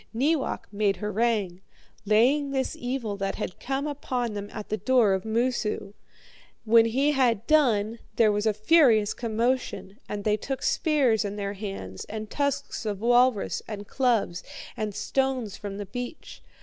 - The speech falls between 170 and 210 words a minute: No, average, 155 wpm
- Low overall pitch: No, high, 225 Hz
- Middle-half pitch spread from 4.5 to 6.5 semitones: No, average, 4.0 semitones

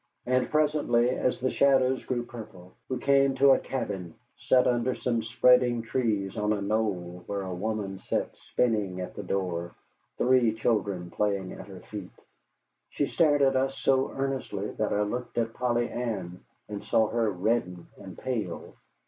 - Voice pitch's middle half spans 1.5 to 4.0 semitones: No, average, 4.4 semitones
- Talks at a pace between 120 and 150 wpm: No, average, 165 wpm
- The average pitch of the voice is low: Yes, low, 115 Hz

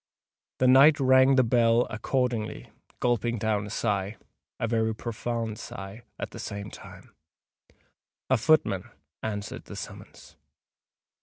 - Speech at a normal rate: No, slow, 110 wpm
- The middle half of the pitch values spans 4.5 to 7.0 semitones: No, average, 3.1 semitones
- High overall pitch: No, low, 115 Hz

